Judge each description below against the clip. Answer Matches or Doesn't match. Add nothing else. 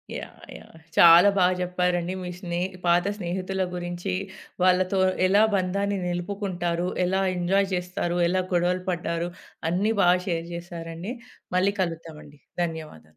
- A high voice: Doesn't match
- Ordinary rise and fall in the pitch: Doesn't match